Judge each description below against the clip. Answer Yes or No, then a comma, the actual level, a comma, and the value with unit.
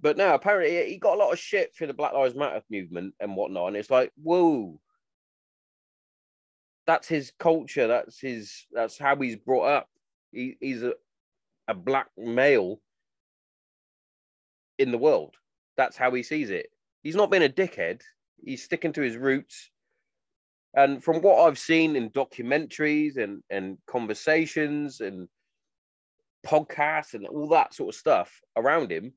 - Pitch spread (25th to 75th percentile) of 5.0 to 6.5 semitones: Yes, wide, 5.5 semitones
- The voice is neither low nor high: Yes, medium, 150 Hz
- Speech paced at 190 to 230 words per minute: No, average, 155 wpm